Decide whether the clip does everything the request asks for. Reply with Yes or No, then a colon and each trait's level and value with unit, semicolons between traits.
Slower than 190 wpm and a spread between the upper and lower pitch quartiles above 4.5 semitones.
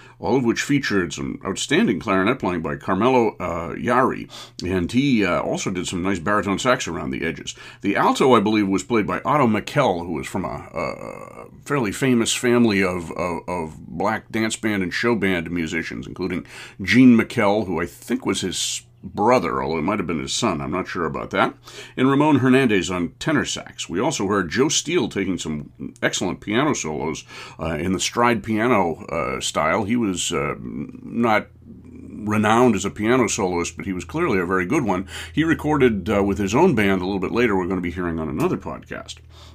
No: average, 200 wpm; average, 5.2 semitones